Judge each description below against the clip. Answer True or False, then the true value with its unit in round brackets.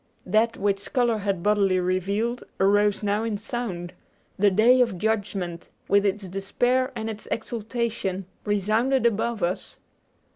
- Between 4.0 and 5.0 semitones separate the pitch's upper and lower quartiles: False (2.9 semitones)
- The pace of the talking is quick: False (135 wpm)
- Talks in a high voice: True (205 Hz)